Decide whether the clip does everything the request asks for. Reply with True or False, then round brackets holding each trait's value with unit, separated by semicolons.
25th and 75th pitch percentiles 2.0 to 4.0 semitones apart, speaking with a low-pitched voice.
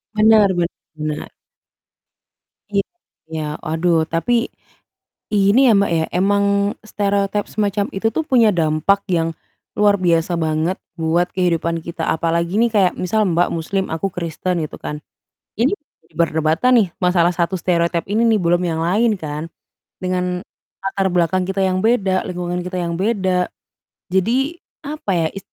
False (3.1 semitones; 180 Hz)